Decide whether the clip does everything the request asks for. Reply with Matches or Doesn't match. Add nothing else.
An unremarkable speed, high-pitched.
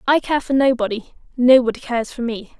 Matches